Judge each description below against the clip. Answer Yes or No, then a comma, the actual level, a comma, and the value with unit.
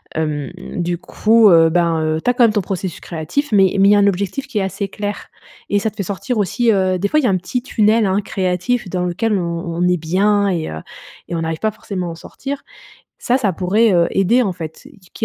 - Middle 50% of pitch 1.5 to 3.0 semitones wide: No, average, 3.7 semitones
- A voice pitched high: Yes, high, 195 Hz